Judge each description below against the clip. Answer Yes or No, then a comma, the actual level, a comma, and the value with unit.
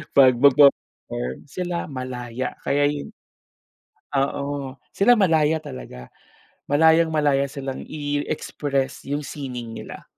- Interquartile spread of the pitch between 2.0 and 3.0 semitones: Yes, narrow, 2.5 semitones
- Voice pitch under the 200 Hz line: Yes, medium, 140 Hz